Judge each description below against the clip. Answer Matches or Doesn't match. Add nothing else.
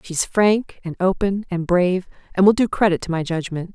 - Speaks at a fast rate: Matches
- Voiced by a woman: Matches